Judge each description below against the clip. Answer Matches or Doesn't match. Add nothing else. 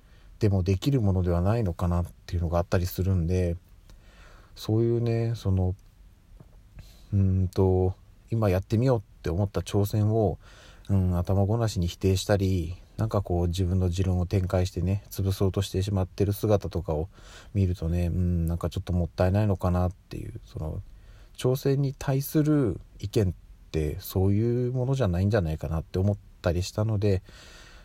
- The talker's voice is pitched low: Matches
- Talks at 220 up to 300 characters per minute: Doesn't match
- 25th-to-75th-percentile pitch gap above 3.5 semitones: Doesn't match